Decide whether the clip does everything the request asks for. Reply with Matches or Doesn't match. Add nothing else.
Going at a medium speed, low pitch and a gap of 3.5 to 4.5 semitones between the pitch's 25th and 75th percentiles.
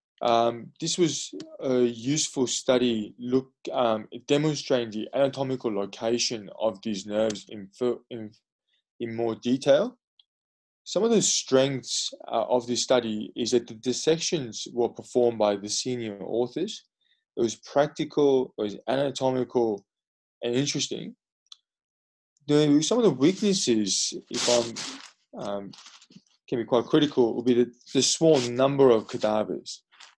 Doesn't match